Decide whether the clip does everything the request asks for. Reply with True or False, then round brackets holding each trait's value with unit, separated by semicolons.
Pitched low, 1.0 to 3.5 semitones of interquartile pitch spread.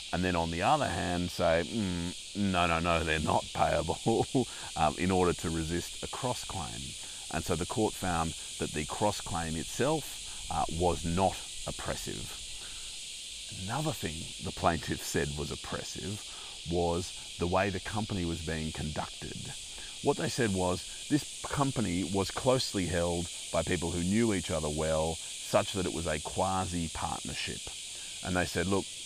True (90 Hz; 2.9 semitones)